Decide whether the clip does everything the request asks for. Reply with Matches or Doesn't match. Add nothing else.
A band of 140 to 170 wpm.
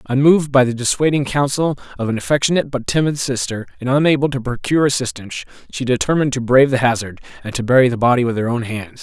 Doesn't match